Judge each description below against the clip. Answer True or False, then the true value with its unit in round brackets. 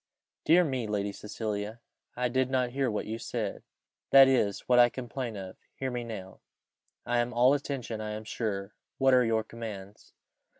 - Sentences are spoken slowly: False (175 wpm)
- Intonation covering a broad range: False (3.2 semitones)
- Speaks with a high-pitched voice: False (120 Hz)